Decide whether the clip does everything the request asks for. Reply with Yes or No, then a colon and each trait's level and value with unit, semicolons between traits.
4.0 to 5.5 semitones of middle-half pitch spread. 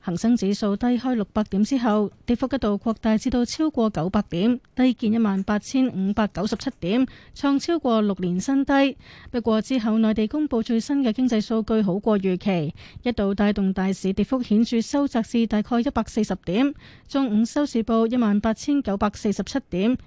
No: average, 3.5 semitones